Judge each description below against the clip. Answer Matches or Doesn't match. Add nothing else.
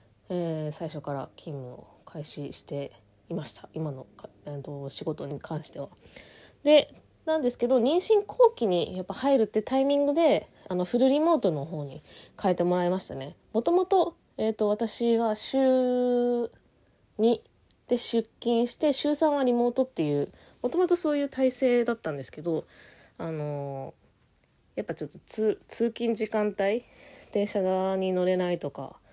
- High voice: Matches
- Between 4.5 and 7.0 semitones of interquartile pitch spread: Doesn't match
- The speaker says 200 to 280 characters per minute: Matches